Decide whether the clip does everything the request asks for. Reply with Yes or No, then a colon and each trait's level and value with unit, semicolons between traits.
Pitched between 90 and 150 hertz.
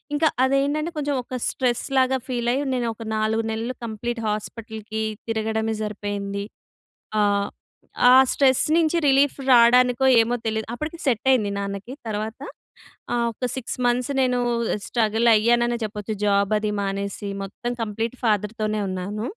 No: high, 225 Hz